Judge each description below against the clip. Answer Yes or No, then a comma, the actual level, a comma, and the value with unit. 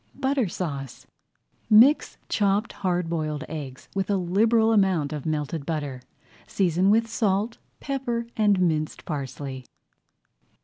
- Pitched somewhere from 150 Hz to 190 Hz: Yes, medium, 185 Hz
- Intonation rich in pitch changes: Yes, wide, 6.2 semitones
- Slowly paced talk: Yes, slow, 120 wpm